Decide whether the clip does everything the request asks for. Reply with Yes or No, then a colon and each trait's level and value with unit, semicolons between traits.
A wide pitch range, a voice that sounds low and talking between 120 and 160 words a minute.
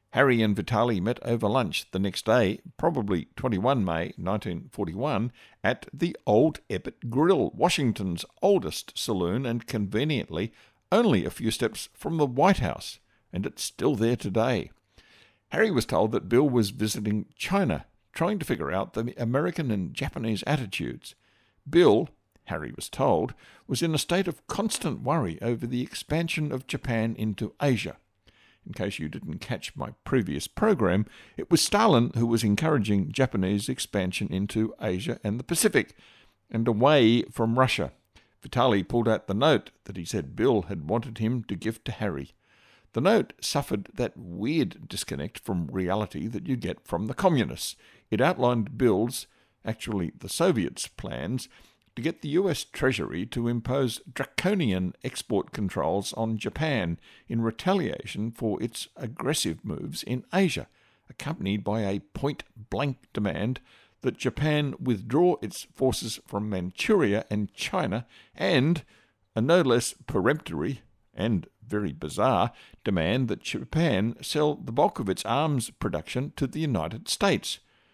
No: average, 4.7 semitones; low, 115 Hz; average, 145 wpm